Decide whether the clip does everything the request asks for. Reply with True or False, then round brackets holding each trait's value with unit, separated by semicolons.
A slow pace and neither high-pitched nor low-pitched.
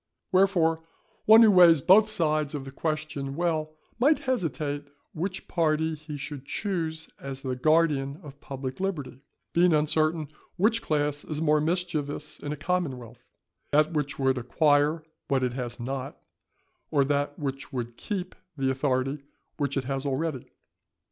False (150 wpm; 150 Hz)